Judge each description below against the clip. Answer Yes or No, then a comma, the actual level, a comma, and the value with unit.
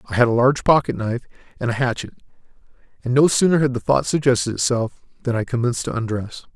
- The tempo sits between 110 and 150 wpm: No, average, 200 wpm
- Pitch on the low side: Yes, low, 125 Hz